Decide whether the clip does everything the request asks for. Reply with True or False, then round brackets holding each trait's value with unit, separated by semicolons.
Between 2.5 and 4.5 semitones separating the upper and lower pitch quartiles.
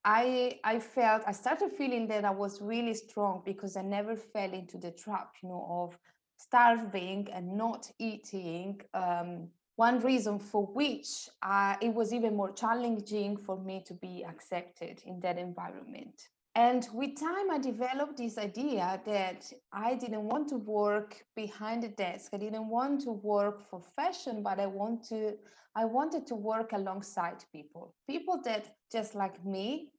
True (3.4 semitones)